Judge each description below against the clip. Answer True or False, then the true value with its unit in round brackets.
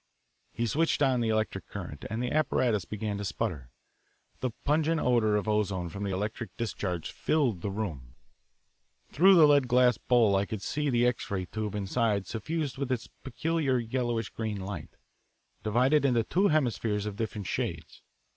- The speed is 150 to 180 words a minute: True (165 wpm)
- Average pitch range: True (4.3 semitones)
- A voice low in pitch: True (115 Hz)